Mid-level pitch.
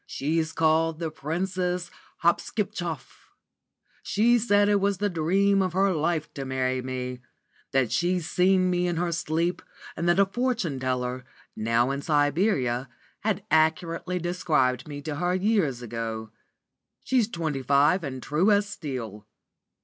Yes: medium, 165 Hz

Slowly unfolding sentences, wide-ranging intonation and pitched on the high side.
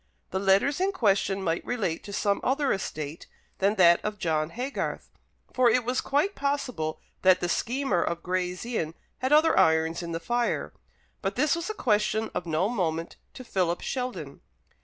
No: average, 175 wpm; wide, 6.8 semitones; high, 200 Hz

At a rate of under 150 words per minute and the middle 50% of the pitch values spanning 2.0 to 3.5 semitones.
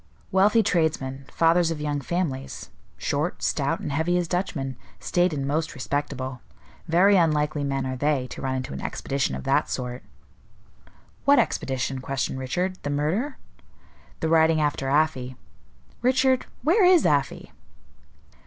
No: average, 140 wpm; average, 4.7 semitones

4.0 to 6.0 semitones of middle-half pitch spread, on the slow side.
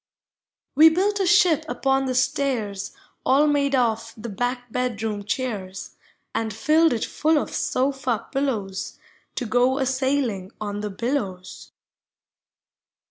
Yes: average, 4.6 semitones; slow, 130 wpm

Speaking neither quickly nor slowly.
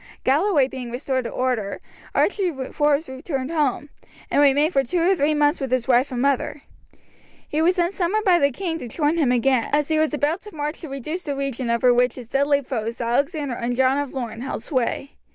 No: fast, 210 wpm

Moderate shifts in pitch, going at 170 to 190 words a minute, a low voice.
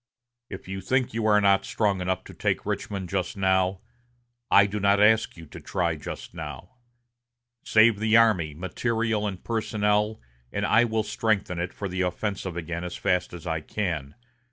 Yes: average, 3.3 semitones; average, 175 wpm; low, 100 Hz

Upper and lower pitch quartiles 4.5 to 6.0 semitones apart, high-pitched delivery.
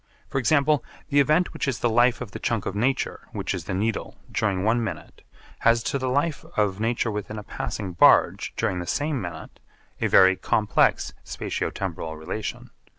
No: average, 5.0 semitones; low, 110 Hz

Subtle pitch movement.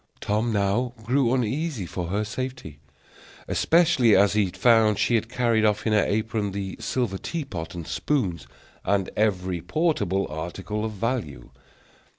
No: average, 4.2 semitones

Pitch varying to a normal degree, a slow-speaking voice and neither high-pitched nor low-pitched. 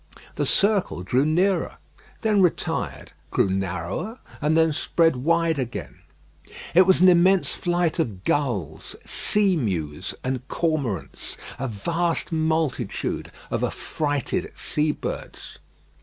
No: wide, 6.5 semitones; slow, 110 wpm; medium, 155 Hz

